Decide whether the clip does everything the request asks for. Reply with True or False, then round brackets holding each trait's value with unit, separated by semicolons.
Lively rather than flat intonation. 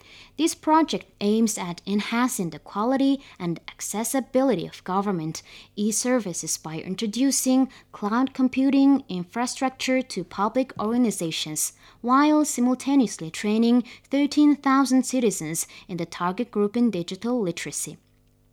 True (6.4 semitones)